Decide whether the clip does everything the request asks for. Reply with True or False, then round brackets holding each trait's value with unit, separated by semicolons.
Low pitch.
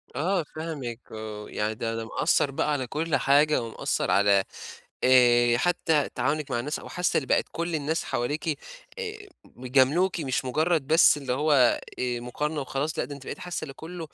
False (145 Hz)